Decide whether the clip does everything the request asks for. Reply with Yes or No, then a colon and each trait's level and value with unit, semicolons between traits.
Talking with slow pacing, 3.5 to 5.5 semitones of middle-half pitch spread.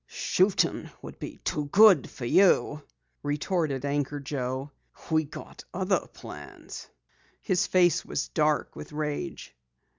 Yes: slow, 120 wpm; average, 4.2 semitones